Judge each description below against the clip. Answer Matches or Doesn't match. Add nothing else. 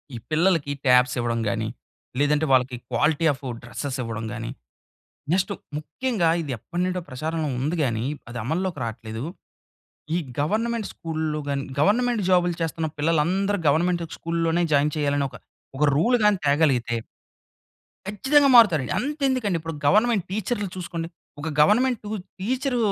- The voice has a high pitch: Doesn't match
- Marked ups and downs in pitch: Matches